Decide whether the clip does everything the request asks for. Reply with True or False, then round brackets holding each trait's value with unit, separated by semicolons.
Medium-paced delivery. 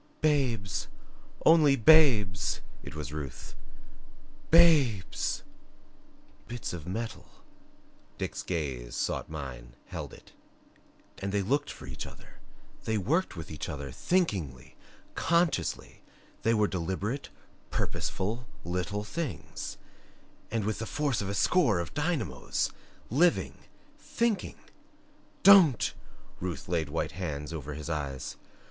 False (115 wpm)